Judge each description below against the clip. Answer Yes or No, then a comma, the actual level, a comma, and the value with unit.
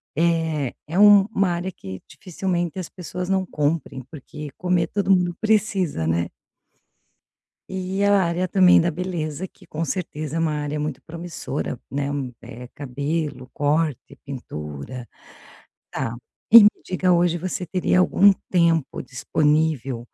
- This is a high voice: No, medium, 165 Hz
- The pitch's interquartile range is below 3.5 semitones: No, average, 4.2 semitones